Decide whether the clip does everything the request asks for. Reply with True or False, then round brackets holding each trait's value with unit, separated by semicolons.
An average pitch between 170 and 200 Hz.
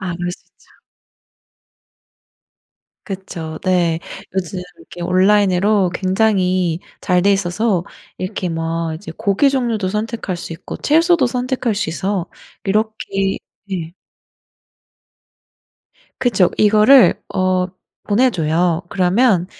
True (190 Hz)